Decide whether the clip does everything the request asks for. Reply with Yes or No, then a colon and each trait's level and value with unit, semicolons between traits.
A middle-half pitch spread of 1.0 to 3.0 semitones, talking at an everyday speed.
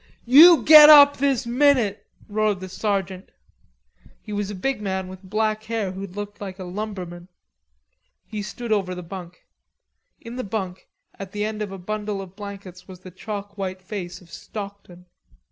Yes: narrow, 2.6 semitones; average, 170 wpm